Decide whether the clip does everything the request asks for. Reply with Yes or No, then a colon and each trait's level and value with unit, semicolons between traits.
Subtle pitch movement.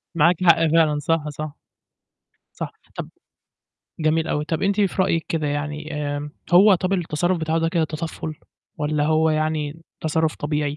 Yes: narrow, 1.8 semitones